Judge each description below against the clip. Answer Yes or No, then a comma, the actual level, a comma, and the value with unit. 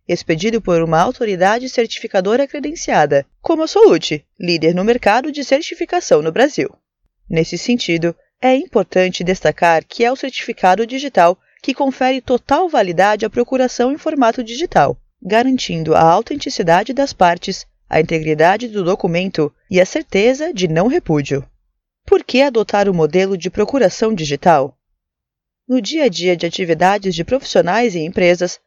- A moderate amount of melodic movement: No, wide, 6.9 semitones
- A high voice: Yes, high, 210 Hz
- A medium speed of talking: Yes, average, 145 wpm